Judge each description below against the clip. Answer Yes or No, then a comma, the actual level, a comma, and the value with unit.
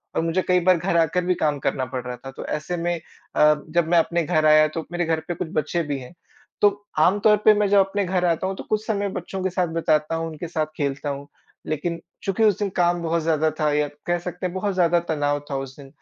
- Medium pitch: Yes, medium, 170 Hz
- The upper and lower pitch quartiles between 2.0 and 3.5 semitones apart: Yes, average, 3.2 semitones